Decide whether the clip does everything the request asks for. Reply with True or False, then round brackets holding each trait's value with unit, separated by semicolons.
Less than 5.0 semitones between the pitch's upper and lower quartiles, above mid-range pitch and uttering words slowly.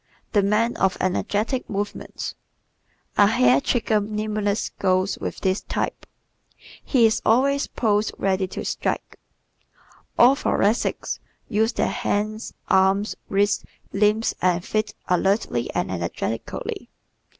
True (2.4 semitones; 205 Hz; 115 wpm)